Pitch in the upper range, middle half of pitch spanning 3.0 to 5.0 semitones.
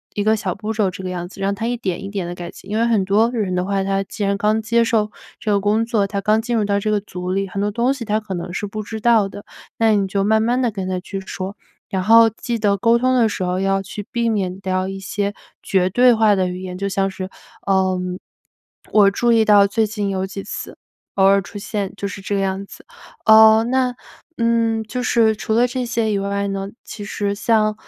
No: high, 205 Hz; narrow, 2.4 semitones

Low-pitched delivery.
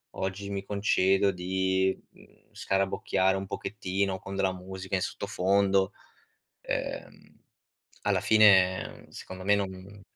Yes: very low, 95 Hz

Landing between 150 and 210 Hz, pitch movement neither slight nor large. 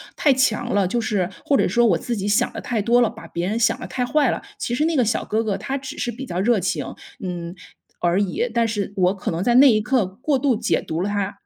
No: high, 220 Hz; average, 4.1 semitones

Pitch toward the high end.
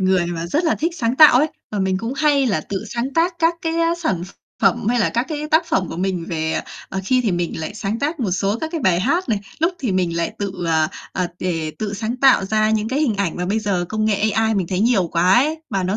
Yes: high, 215 Hz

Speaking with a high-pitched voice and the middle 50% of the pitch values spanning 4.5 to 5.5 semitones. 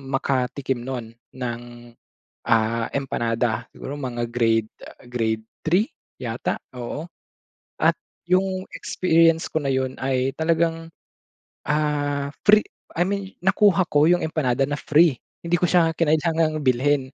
No: medium, 145 Hz; average, 5.1 semitones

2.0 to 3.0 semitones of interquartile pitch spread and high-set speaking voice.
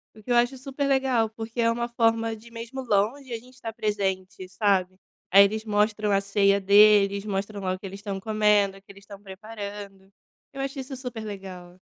Yes: average, 2.7 semitones; high, 210 Hz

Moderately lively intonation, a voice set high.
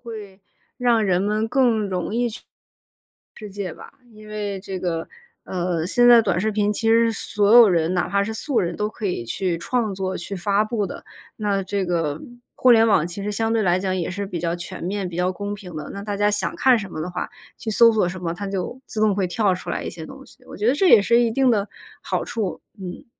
Yes: average, 3.4 semitones; high, 200 Hz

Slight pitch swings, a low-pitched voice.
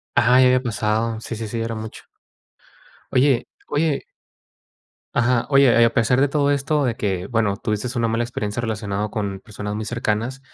No: average, 3.1 semitones; low, 115 Hz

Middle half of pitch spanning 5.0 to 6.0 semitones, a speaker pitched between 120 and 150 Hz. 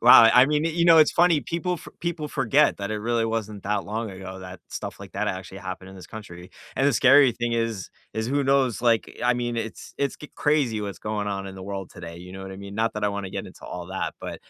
No: wide, 5.6 semitones; low, 110 Hz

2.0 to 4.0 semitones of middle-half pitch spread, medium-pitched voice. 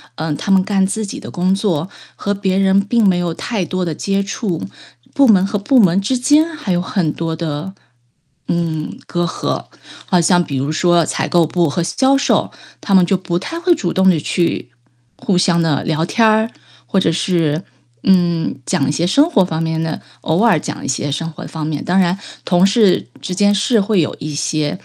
Yes: average, 3.4 semitones; medium, 180 Hz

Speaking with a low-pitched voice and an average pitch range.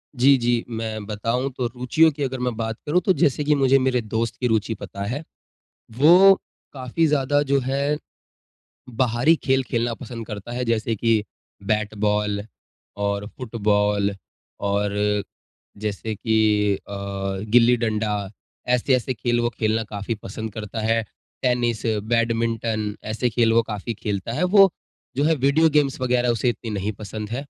Yes: low, 115 Hz; average, 3.2 semitones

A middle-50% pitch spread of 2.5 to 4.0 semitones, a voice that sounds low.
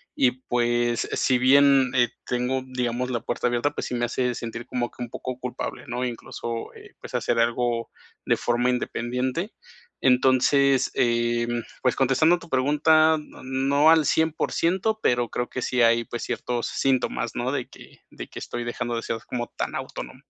No: narrow, 2.0 semitones; low, 125 Hz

